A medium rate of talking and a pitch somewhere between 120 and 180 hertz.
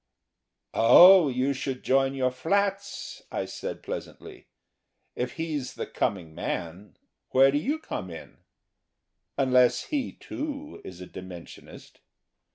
No: slow, 120 wpm; low, 135 Hz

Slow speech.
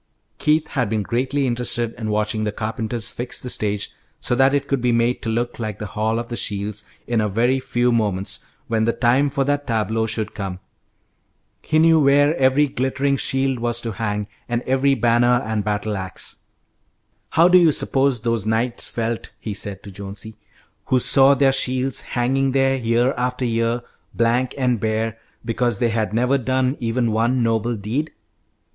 No: average, 180 wpm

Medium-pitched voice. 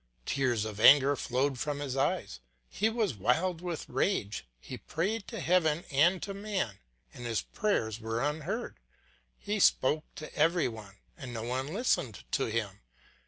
Yes: medium, 145 Hz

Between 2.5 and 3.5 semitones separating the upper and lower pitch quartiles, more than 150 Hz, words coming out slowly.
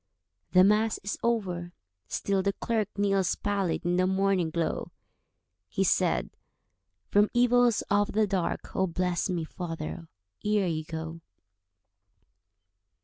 Yes: average, 3.2 semitones; high, 190 Hz; slow, 120 wpm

